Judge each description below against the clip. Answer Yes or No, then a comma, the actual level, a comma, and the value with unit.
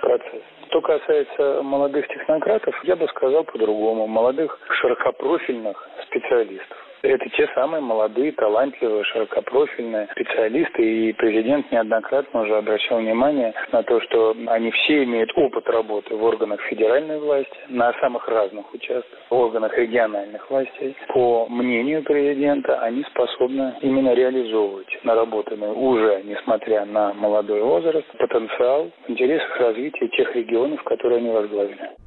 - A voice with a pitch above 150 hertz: No, low, 135 Hz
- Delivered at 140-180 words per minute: No, average, 125 wpm